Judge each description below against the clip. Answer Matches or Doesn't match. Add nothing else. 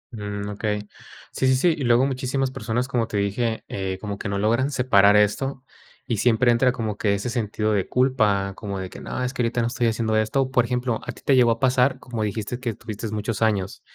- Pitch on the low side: Matches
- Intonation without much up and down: Doesn't match